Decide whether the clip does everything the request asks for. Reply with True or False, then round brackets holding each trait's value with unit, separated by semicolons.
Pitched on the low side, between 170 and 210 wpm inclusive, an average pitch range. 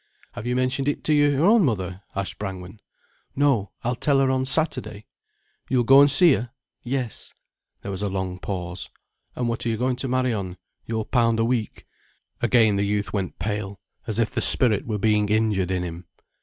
True (115 Hz; 185 wpm; 4.5 semitones)